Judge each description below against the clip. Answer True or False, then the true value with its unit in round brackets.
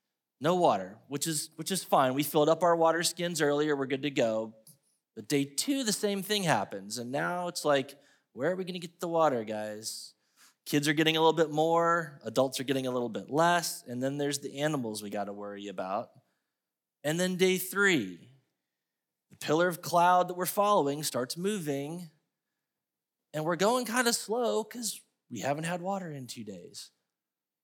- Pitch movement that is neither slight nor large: True (4.5 semitones)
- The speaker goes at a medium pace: True (195 wpm)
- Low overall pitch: False (155 Hz)